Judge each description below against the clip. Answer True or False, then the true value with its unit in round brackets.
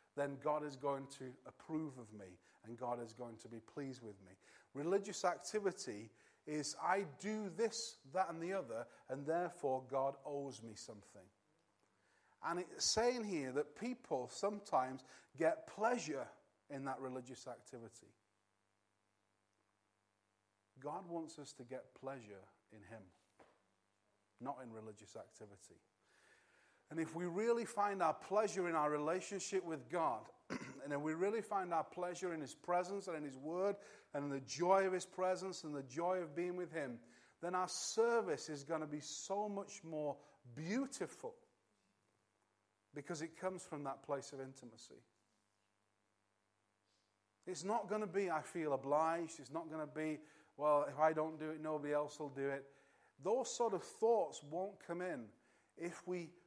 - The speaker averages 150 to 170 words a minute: True (160 wpm)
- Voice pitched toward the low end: False (150 Hz)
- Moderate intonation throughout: False (7.3 semitones)